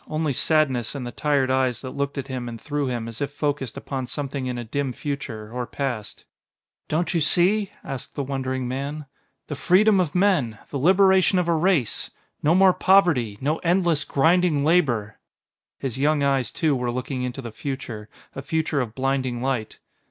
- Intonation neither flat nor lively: Yes, average, 4.0 semitones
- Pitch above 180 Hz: No, medium, 140 Hz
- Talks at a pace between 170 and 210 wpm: Yes, average, 180 wpm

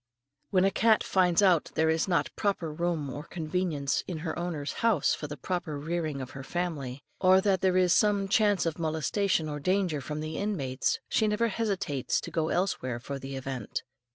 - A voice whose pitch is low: No, medium, 170 Hz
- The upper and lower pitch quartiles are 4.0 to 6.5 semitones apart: Yes, average, 4.5 semitones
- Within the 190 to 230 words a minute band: Yes, average, 195 wpm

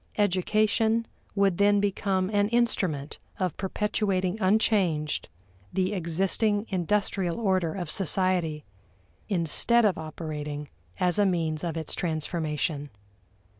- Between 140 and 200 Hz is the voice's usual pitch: Yes, medium, 185 Hz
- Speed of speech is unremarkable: No, slow, 105 wpm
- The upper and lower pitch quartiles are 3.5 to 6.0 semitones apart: Yes, average, 4.0 semitones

